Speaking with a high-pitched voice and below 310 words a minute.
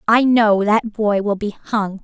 Yes: high, 210 Hz; fast, 205 wpm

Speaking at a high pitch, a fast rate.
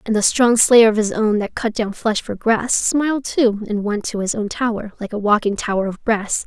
Yes: high, 220 Hz; fast, 250 wpm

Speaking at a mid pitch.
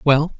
Yes: medium, 145 Hz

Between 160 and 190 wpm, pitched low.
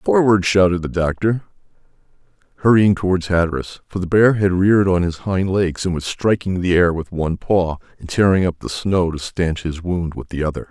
No: average, 200 wpm; very low, 90 Hz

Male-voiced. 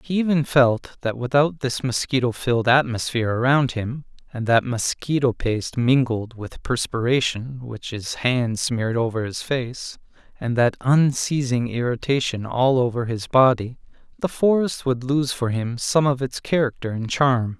Yes: male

